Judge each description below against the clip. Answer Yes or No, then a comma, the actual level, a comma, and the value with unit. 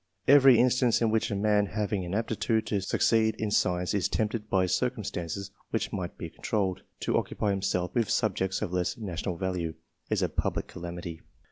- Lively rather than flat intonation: No, average, 3.5 semitones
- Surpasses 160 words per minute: Yes, average, 180 wpm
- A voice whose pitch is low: Yes, low, 100 Hz